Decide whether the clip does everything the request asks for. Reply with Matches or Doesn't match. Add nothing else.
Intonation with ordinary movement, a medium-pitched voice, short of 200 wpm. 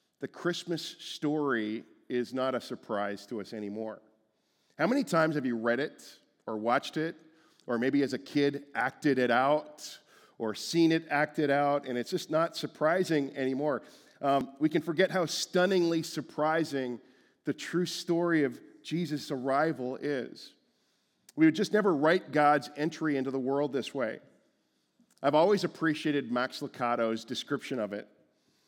Matches